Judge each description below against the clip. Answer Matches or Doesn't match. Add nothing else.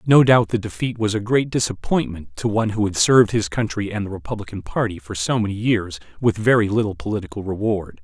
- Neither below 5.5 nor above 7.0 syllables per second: Matches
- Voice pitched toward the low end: Matches